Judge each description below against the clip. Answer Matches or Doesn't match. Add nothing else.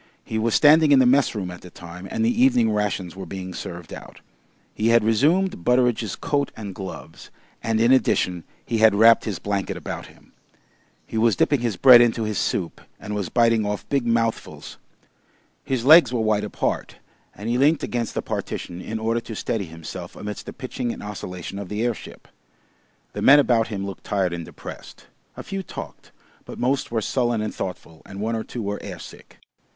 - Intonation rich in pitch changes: Doesn't match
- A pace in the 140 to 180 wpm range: Doesn't match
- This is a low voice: Matches